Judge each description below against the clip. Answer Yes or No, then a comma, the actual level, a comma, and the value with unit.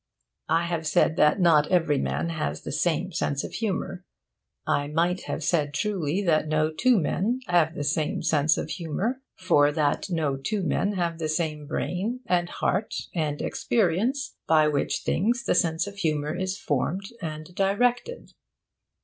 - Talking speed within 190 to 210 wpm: No, average, 165 wpm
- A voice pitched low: No, medium, 170 Hz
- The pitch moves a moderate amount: Yes, average, 4.2 semitones